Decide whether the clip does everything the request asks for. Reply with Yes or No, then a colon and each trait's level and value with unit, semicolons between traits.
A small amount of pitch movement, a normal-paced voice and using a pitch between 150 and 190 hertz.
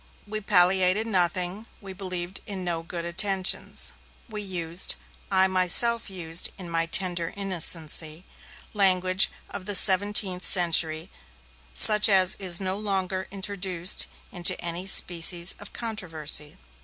No: narrow, 2.2 semitones; slow, 125 wpm; medium, 185 Hz